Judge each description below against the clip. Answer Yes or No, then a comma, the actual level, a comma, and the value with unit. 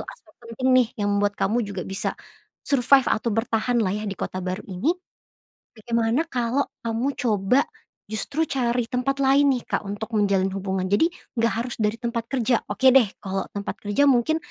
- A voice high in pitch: Yes, high, 230 Hz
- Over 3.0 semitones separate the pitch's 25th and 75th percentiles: Yes, average, 4.1 semitones